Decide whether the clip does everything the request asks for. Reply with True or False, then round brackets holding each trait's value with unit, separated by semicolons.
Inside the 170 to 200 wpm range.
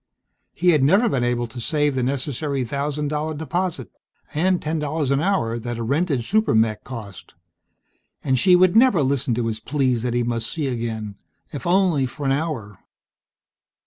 True (175 wpm)